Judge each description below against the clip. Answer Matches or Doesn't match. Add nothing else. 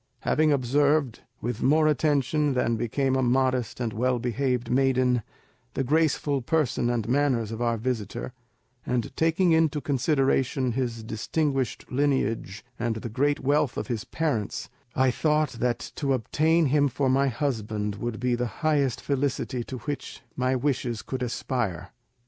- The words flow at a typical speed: Matches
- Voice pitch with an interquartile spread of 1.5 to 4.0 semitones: Matches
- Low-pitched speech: Matches